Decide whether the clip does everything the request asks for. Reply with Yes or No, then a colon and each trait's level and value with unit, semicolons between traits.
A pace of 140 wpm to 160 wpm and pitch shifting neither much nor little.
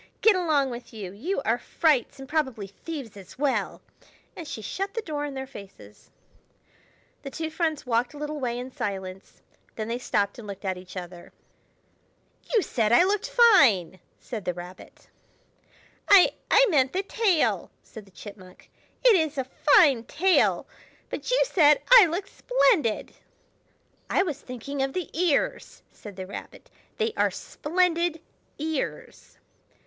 No: average, 155 wpm; wide, 8.1 semitones